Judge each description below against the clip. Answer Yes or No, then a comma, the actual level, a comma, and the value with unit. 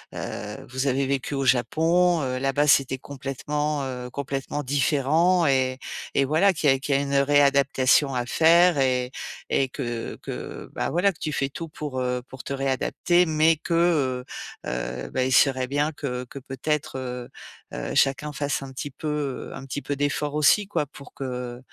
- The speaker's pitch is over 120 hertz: Yes, medium, 140 Hz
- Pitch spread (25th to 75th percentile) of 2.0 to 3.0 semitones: Yes, narrow, 2.6 semitones